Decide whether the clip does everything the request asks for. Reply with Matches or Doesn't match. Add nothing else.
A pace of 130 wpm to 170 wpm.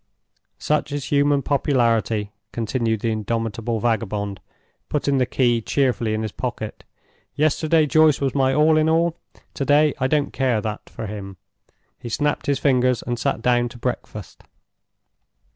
Matches